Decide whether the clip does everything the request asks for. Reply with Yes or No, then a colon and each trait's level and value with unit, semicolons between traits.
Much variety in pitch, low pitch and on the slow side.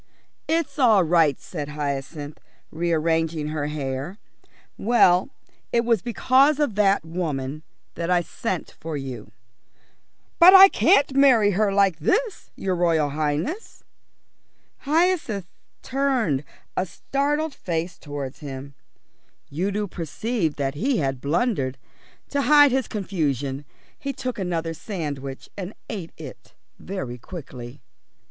No: wide, 8.4 semitones; medium, 175 Hz; slow, 120 wpm